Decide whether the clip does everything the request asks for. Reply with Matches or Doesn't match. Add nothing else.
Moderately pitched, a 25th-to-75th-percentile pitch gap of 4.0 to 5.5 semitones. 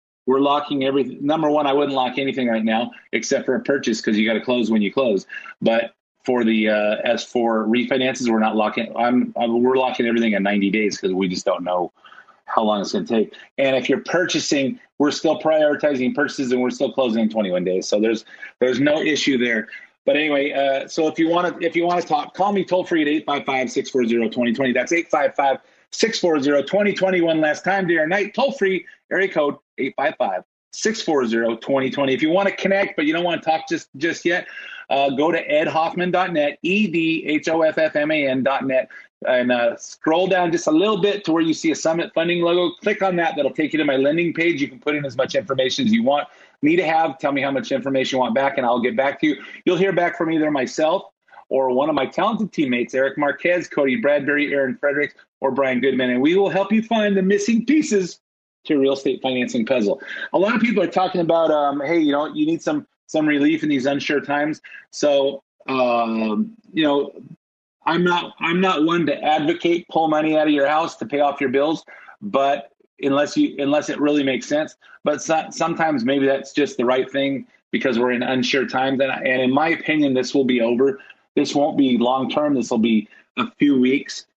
Matches